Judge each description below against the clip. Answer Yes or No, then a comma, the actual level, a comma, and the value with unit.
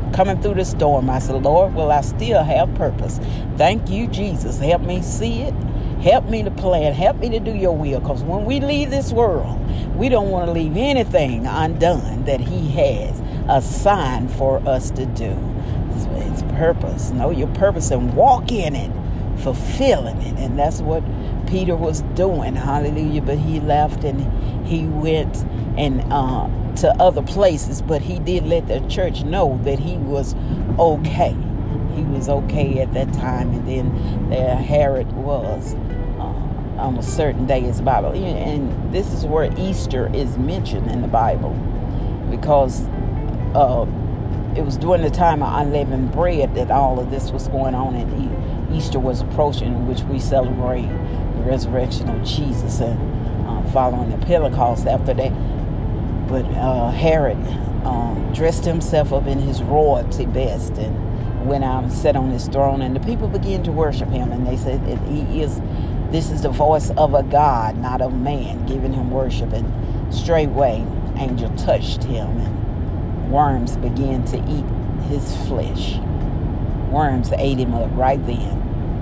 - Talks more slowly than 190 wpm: Yes, average, 165 wpm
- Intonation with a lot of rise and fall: No, average, 3.5 semitones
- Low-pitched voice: Yes, low, 125 Hz